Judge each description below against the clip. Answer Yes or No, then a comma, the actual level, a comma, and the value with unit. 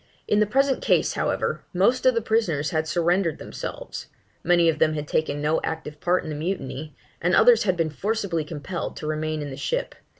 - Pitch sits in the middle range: Yes, medium, 165 Hz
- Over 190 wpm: Yes, average, 200 wpm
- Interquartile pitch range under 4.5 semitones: No, average, 4.8 semitones